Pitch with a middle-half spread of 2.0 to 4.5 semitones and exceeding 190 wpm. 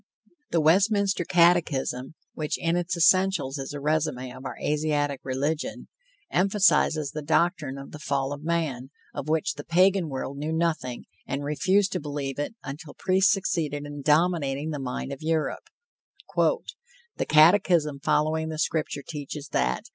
No: average, 3.4 semitones; average, 150 wpm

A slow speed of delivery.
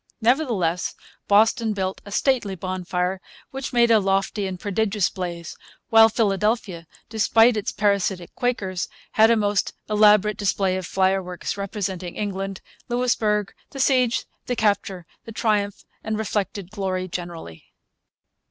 Yes: slow, 125 wpm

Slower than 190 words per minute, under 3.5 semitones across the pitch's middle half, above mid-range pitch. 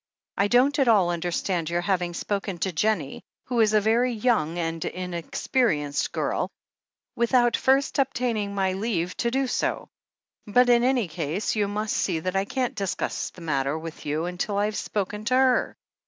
No: average, 170 wpm; wide, 5.5 semitones; high, 200 Hz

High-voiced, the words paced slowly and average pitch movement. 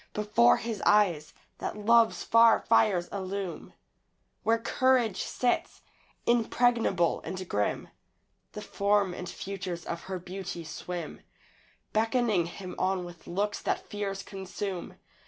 Yes: high, 195 Hz; slow, 120 wpm; average, 3.6 semitones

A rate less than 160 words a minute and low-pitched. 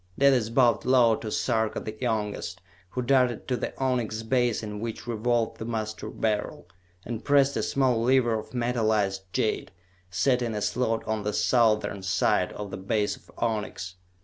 No: average, 170 wpm; low, 115 Hz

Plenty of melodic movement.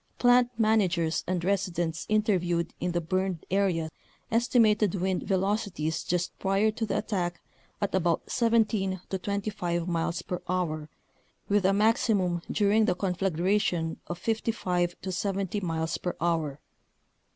No: average, 3.1 semitones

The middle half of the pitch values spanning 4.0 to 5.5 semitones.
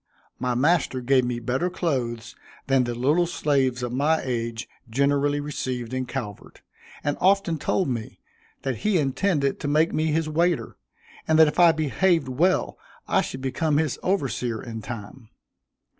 Yes: average, 4.5 semitones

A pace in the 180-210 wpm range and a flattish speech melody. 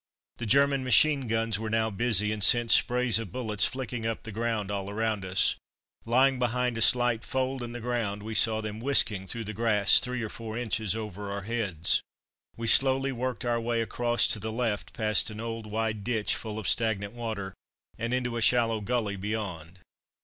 Yes: average, 195 wpm; narrow, 2.3 semitones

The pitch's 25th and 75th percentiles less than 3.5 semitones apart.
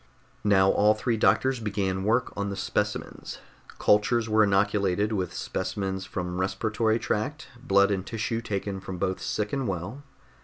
Yes: narrow, 2.4 semitones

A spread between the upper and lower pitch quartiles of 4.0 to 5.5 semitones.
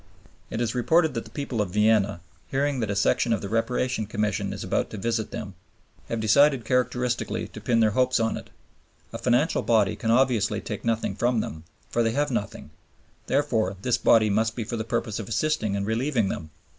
No: average, 2.9 semitones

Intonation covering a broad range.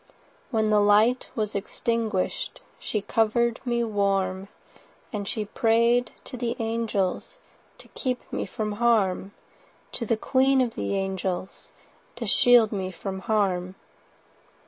No: average, 3.1 semitones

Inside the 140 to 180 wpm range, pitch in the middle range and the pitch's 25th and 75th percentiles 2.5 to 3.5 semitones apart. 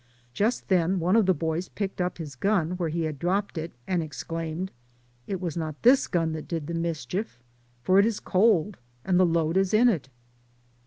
No: average, 200 wpm; medium, 175 Hz; average, 3.1 semitones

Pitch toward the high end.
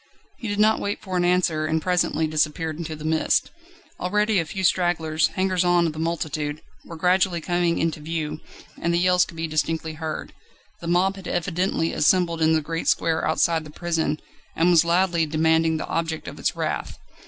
No: medium, 165 Hz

